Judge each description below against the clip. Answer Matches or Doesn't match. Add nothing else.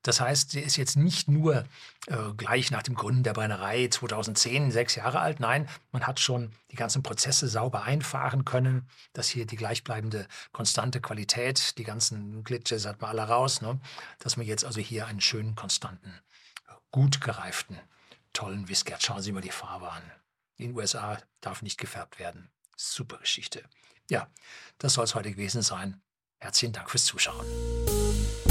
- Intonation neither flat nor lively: Matches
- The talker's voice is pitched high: Doesn't match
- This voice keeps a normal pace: Matches